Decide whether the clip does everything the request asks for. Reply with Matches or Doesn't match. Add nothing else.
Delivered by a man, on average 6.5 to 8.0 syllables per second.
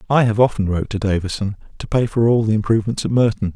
Matches